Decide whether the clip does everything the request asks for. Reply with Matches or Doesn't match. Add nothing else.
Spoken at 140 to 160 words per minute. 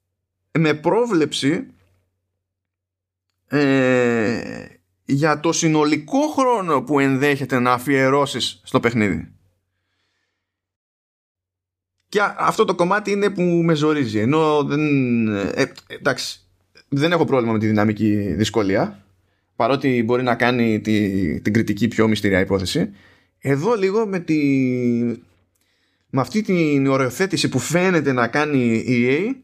Doesn't match